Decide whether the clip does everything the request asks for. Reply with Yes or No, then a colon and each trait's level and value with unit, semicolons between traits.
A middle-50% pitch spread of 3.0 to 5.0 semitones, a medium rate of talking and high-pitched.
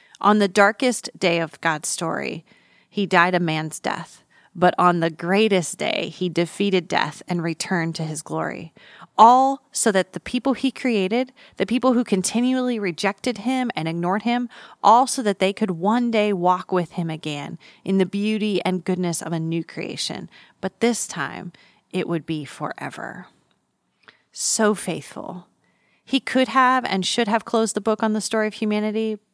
Yes: average, 4.4 semitones; average, 170 wpm; high, 200 Hz